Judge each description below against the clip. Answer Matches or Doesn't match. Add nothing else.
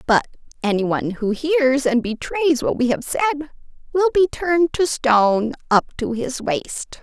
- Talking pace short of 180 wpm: Matches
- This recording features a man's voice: Doesn't match